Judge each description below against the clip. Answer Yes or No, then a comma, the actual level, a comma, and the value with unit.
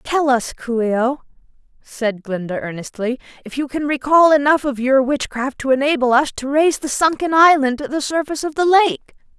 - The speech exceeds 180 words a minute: Yes, average, 190 wpm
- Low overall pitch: No, very high, 270 Hz